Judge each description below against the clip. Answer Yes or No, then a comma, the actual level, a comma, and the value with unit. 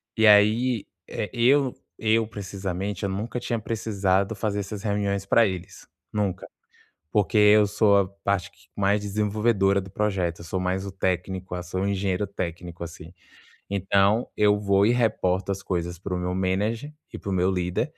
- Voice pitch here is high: No, low, 100 Hz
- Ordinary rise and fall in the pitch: No, narrow, 2.2 semitones